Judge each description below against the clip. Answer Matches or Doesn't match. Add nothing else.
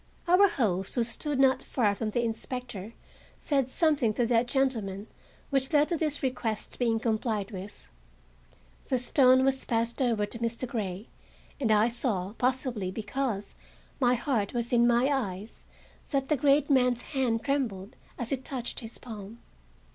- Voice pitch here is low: Doesn't match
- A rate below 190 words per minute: Matches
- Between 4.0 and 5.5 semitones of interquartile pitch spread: Doesn't match